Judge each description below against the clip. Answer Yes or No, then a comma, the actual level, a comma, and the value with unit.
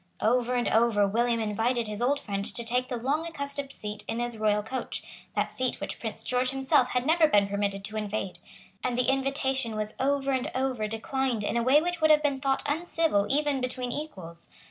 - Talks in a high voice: Yes, very high, 250 Hz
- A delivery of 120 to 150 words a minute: No, fast, 205 wpm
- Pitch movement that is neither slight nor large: Yes, average, 4.1 semitones